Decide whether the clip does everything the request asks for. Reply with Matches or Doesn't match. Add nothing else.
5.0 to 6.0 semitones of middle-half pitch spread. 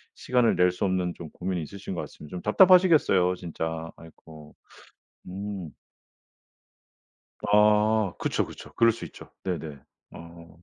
Doesn't match